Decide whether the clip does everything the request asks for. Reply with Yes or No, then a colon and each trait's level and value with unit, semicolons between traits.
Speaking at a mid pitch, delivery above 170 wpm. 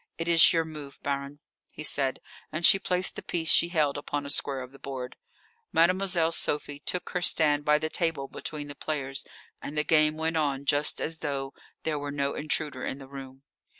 Yes: medium, 150 Hz; average, 200 wpm